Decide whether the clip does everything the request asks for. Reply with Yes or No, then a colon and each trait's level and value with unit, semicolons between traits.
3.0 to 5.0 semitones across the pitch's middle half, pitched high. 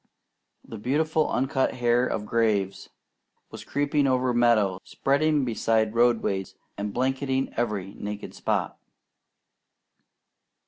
No: average, 3.9 semitones; low, 120 Hz